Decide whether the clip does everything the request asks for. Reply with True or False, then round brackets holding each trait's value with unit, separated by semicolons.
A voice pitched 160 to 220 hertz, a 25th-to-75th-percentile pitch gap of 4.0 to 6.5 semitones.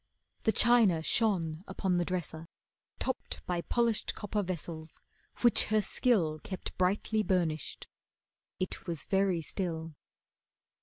True (185 Hz; 4.4 semitones)